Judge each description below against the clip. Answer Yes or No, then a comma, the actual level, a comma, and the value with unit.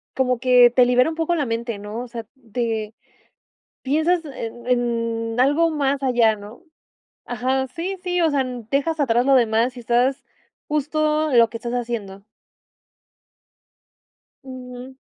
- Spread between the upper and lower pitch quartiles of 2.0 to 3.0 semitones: No, average, 3.4 semitones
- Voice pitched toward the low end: No, very high, 250 Hz